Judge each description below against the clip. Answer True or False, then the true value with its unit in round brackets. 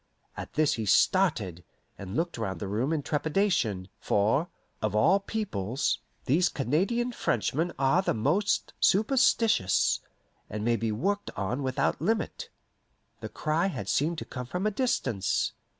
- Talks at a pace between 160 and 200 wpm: False (145 wpm)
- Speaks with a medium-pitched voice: True (150 Hz)